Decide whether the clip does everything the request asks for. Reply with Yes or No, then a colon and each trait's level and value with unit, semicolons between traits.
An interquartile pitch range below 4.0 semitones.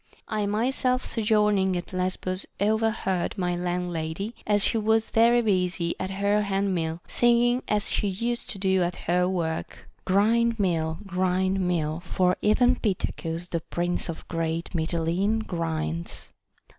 Yes: average, 3.5 semitones